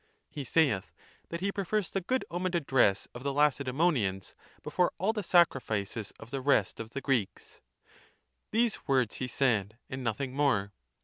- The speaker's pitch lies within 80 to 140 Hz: Yes, low, 135 Hz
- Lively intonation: Yes, wide, 7.6 semitones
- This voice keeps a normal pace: Yes, average, 160 wpm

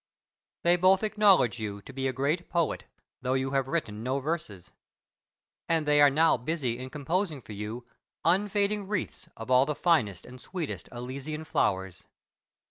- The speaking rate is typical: Yes, average, 160 wpm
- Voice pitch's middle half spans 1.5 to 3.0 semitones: No, wide, 5.5 semitones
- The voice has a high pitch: No, medium, 140 Hz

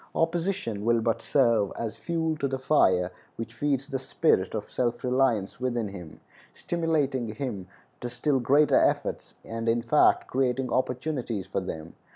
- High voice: No, low, 125 Hz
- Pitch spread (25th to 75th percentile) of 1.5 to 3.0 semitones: No, average, 3.9 semitones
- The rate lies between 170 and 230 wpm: No, average, 155 wpm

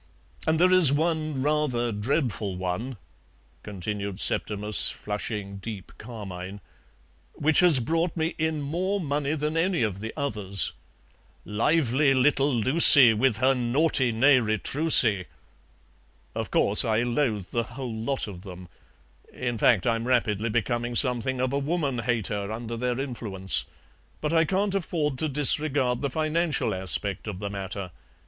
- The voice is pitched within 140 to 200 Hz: No, low, 125 Hz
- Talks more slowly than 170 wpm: Yes, average, 140 wpm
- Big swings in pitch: Yes, wide, 5.9 semitones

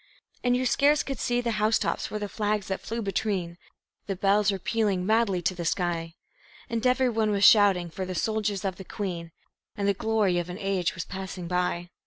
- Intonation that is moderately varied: Yes, average, 3.4 semitones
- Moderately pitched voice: No, high, 200 Hz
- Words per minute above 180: Yes, fast, 205 wpm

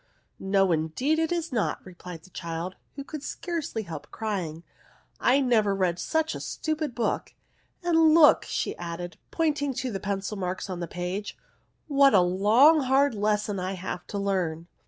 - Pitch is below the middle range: No, high, 205 Hz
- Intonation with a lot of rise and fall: Yes, wide, 7.8 semitones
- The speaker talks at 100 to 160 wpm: No, average, 175 wpm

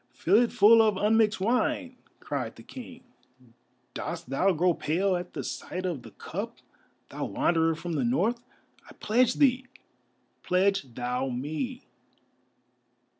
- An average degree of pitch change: No, wide, 6.4 semitones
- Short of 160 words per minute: Yes, slow, 135 wpm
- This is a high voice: Yes, high, 195 Hz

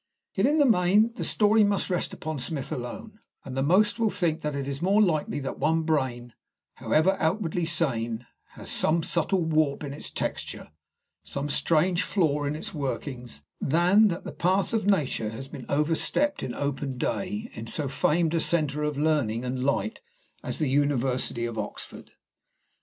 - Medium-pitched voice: Yes, medium, 155 Hz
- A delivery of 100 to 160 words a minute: No, average, 175 wpm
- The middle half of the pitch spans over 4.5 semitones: Yes, average, 5.2 semitones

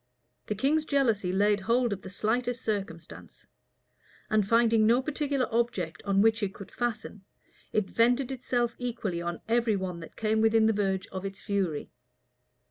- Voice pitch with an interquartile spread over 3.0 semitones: Yes, average, 3.6 semitones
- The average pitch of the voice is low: No, high, 220 Hz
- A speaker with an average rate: Yes, average, 160 wpm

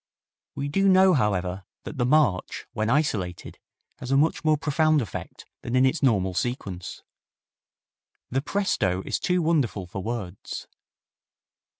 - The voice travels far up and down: Yes, wide, 8.1 semitones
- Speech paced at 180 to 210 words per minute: No, slow, 135 wpm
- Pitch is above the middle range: No, low, 130 Hz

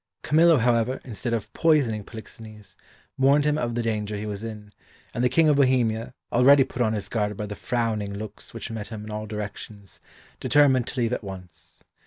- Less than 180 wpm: No, average, 195 wpm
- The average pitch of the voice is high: No, low, 115 Hz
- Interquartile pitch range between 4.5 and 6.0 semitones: No, average, 3.3 semitones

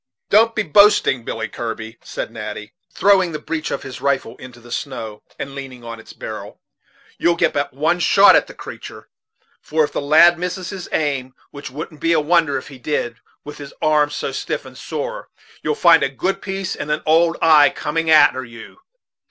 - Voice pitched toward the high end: No, medium, 150 Hz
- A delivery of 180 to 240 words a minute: Yes, average, 195 wpm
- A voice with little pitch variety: No, average, 4.8 semitones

